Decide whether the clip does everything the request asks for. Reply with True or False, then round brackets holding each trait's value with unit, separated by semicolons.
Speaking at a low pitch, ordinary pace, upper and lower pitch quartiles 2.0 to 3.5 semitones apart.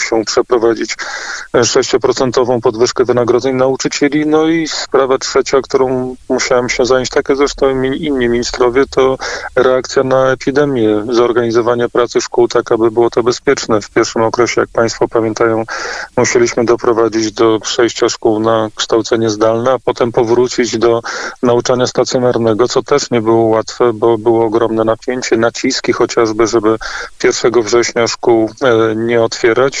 True (120 Hz; 140 wpm; 2.8 semitones)